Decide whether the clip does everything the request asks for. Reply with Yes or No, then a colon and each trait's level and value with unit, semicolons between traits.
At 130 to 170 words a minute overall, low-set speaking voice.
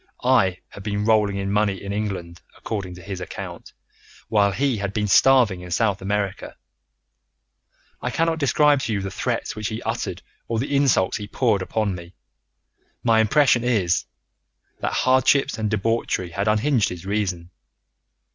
Yes: average, 160 wpm; low, 105 Hz